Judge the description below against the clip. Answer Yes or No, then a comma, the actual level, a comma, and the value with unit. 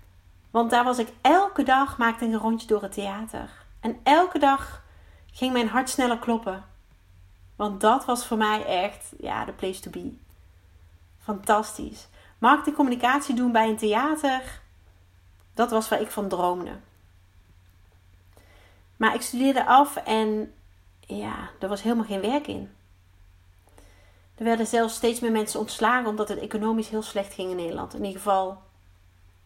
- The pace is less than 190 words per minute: Yes, average, 155 wpm